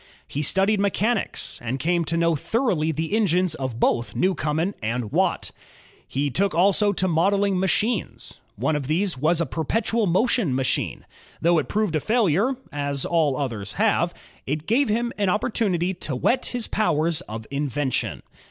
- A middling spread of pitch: No, wide, 5.8 semitones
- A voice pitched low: No, medium, 170 Hz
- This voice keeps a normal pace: Yes, average, 155 wpm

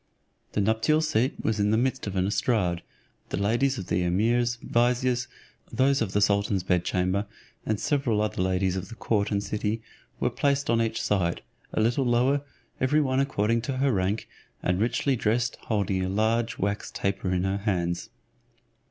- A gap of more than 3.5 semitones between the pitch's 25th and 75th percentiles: Yes, average, 3.9 semitones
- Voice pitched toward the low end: Yes, low, 110 Hz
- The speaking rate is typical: Yes, average, 180 wpm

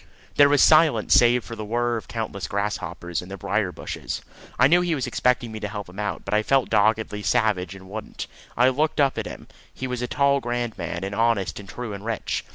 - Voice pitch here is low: Yes, low, 110 Hz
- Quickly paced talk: Yes, fast, 235 wpm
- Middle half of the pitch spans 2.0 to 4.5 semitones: Yes, average, 3.6 semitones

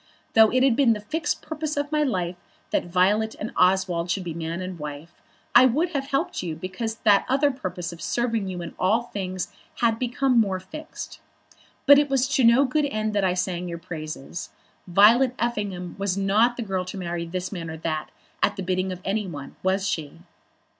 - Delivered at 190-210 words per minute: Yes, average, 200 wpm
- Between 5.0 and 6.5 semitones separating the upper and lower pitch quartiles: Yes, average, 5.3 semitones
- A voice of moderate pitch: No, high, 195 Hz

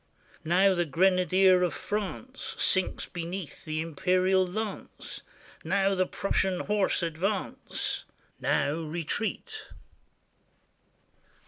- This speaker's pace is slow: Yes, slow, 90 wpm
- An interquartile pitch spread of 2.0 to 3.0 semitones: Yes, narrow, 2.5 semitones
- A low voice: No, medium, 185 Hz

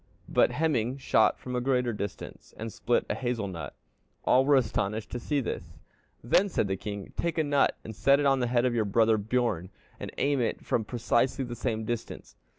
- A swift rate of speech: Yes, fast, 210 wpm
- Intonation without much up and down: No, average, 3.4 semitones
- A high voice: No, low, 120 Hz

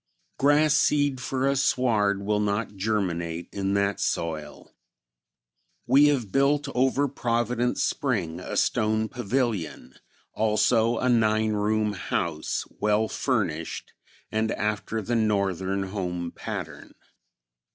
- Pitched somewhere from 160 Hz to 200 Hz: No, low, 110 Hz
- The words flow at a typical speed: No, slow, 110 wpm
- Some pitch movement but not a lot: Yes, average, 4.1 semitones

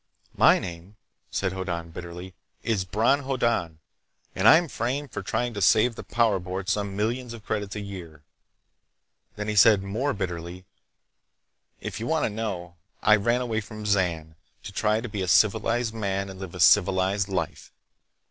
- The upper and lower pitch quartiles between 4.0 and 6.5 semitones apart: No, average, 3.4 semitones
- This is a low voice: Yes, low, 100 Hz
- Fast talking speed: No, average, 165 wpm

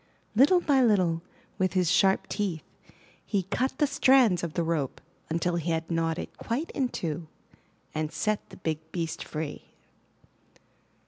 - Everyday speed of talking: Yes, average, 150 wpm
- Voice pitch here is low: No, medium, 175 Hz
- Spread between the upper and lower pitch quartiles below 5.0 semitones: No, wide, 5.5 semitones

